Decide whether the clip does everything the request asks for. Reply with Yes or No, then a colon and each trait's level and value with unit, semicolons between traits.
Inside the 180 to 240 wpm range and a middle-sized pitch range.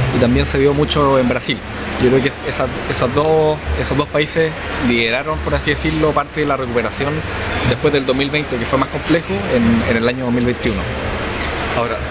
No: average, 170 wpm; average, 3.5 semitones